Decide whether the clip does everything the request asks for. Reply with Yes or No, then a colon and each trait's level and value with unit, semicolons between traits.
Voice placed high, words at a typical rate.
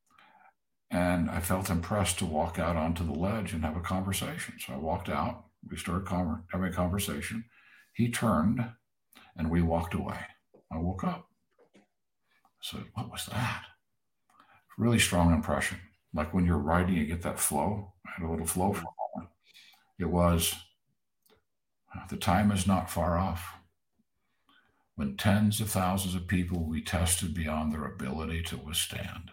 No: very low, 90 Hz; average, 160 wpm